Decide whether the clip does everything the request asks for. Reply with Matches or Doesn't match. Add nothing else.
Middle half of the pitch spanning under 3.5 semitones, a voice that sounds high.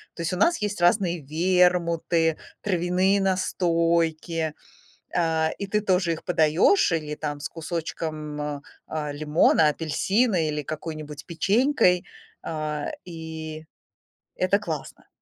Doesn't match